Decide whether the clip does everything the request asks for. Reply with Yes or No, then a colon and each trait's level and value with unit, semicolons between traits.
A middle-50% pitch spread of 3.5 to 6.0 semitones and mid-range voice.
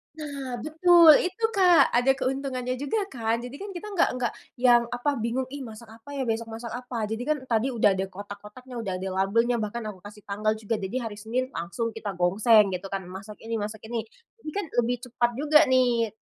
No: average, 3.8 semitones; high, 235 Hz